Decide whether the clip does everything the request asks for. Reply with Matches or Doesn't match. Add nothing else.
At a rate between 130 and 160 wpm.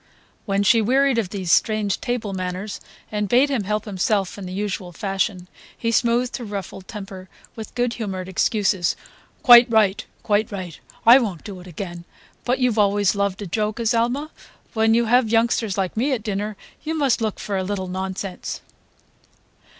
Doesn't match